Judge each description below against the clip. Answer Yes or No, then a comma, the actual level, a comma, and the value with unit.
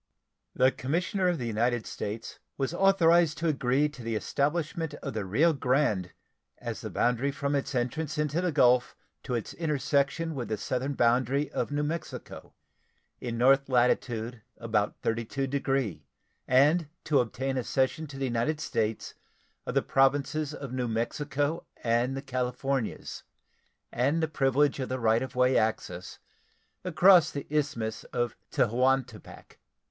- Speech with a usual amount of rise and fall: Yes, average, 3.6 semitones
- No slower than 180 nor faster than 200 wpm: No, average, 145 wpm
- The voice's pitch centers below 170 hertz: Yes, low, 135 Hz